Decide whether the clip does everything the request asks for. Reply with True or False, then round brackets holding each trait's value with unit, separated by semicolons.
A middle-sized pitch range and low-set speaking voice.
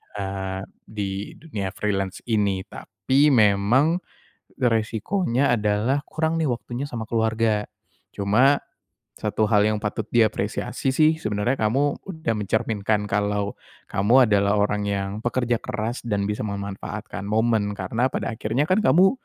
True (3.5 semitones; 110 Hz)